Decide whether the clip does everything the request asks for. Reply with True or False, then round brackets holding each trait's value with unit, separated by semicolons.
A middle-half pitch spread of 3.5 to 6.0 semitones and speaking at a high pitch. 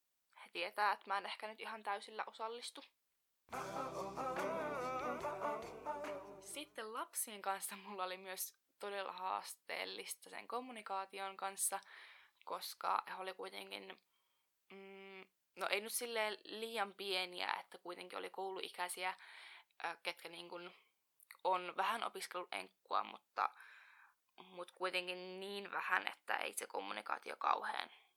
False (2.8 semitones; 195 Hz)